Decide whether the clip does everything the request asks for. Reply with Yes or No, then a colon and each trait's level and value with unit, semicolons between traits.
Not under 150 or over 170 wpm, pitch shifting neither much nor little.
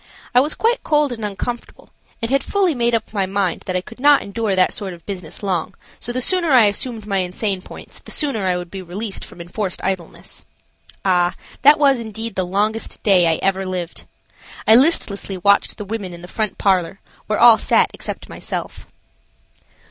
No: average, 195 wpm; average, 4.3 semitones